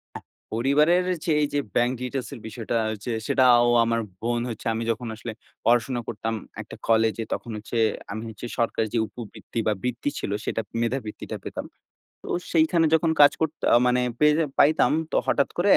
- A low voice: Yes, low, 120 Hz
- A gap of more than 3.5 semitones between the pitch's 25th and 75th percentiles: Yes, average, 4.2 semitones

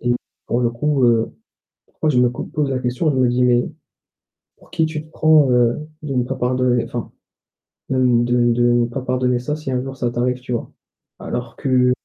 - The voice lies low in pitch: Yes, low, 125 Hz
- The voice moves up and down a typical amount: No, narrow, 1.7 semitones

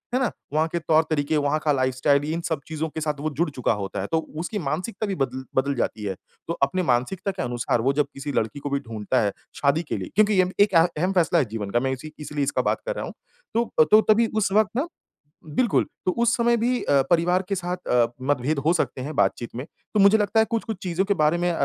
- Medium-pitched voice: Yes, medium, 155 Hz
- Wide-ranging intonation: Yes, wide, 5.8 semitones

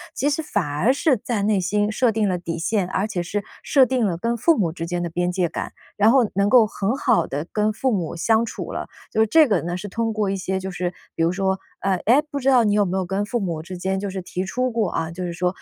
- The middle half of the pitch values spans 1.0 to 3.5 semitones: No, average, 4.0 semitones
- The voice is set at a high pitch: Yes, high, 200 Hz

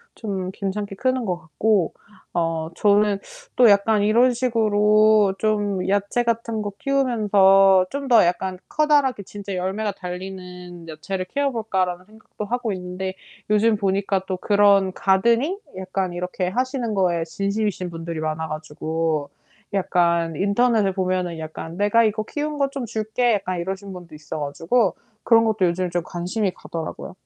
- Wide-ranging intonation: No, average, 3.4 semitones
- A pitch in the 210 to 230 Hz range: No, high, 195 Hz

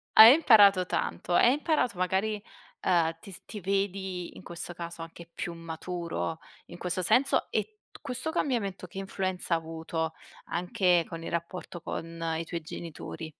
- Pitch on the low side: No, medium, 180 Hz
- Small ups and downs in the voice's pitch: No, average, 3.1 semitones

